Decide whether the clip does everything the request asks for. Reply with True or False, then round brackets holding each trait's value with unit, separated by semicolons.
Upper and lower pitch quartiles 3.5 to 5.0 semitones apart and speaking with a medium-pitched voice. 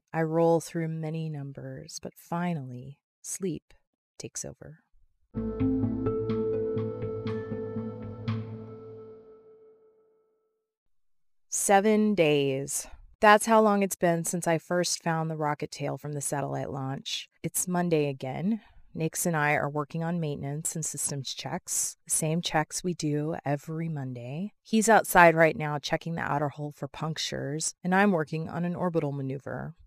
True (4.6 semitones; 155 Hz)